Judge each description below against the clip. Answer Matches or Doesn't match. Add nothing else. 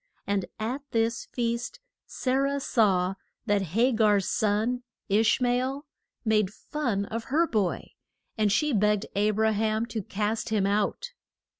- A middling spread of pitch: Matches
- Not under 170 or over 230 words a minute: Doesn't match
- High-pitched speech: Matches